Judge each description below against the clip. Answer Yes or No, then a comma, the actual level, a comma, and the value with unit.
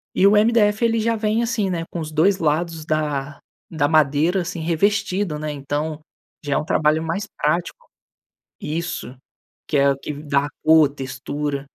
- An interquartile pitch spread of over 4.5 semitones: Yes, average, 5.0 semitones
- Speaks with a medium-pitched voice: Yes, medium, 160 Hz